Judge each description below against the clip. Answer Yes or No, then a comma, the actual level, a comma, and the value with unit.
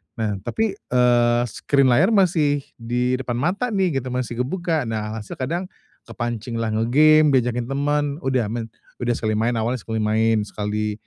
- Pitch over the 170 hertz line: No, low, 120 Hz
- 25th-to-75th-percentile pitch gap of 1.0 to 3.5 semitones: No, average, 4.2 semitones